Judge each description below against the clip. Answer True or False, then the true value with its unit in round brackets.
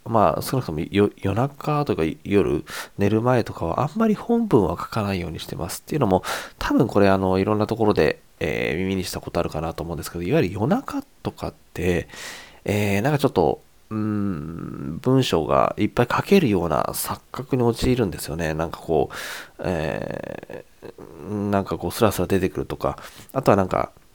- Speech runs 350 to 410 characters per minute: True (370 characters per minute)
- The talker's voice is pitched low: True (100 Hz)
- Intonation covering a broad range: True (5.7 semitones)